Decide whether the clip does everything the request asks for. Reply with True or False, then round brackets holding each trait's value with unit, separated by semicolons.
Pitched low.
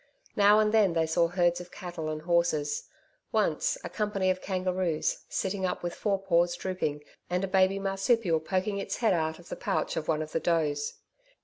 False (180 Hz)